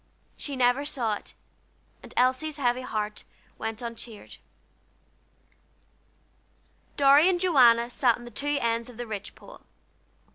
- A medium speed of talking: No, slow, 130 wpm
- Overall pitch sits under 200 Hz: No, high, 245 Hz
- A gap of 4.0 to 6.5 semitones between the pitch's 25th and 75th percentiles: No, average, 3.5 semitones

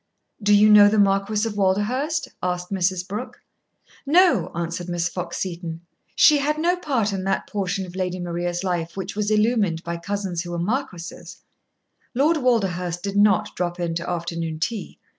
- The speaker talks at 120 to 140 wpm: No, average, 170 wpm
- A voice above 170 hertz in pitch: Yes, high, 190 Hz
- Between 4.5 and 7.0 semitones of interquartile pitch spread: No, average, 3.4 semitones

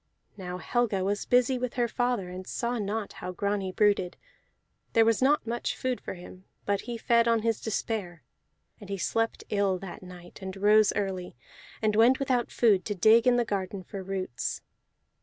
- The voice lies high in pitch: Yes, high, 205 Hz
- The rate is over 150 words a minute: Yes, average, 180 wpm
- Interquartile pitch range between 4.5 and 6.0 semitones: No, average, 3.7 semitones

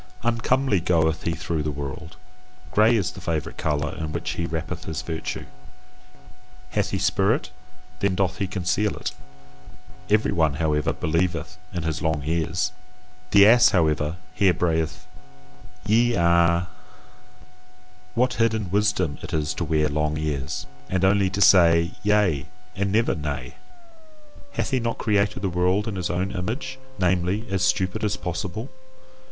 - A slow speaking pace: No, average, 145 wpm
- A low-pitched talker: Yes, very low, 90 Hz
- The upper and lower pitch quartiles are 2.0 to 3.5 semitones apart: No, average, 4.3 semitones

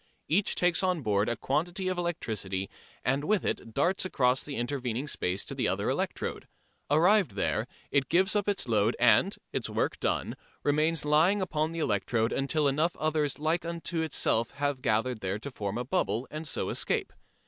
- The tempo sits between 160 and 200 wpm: Yes, average, 180 wpm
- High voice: No, medium, 145 Hz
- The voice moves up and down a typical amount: No, wide, 6.1 semitones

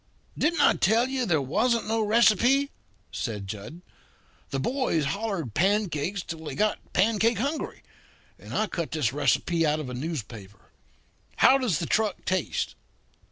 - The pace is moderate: Yes, average, 150 wpm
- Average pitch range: No, wide, 7.1 semitones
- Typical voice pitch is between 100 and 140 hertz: No, medium, 185 Hz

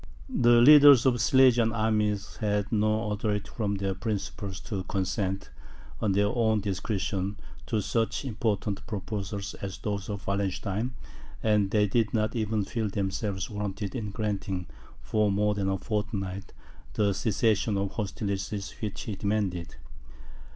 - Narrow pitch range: Yes, narrow, 1.9 semitones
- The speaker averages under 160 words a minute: Yes, average, 140 wpm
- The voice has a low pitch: Yes, low, 105 Hz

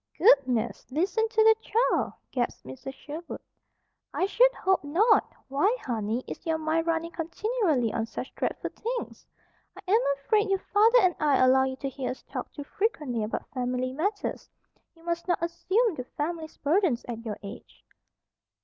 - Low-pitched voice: No, very high, 320 Hz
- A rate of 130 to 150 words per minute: No, average, 165 wpm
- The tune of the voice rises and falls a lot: Yes, wide, 7.4 semitones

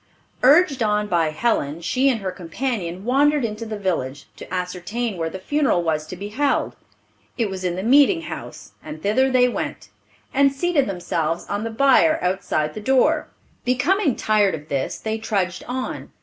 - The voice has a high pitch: Yes, high, 215 Hz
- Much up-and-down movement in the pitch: Yes, wide, 6.6 semitones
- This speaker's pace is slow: No, average, 175 wpm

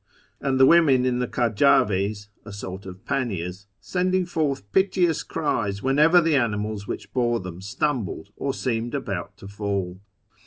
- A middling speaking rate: Yes, average, 145 wpm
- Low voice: Yes, low, 120 Hz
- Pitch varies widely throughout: Yes, wide, 5.8 semitones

